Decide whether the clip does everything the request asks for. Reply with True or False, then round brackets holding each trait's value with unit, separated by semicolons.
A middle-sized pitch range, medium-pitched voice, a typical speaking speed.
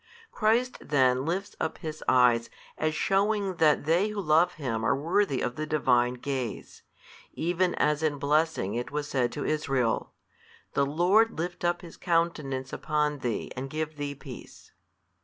True (4.6 semitones; 150 Hz; 160 wpm)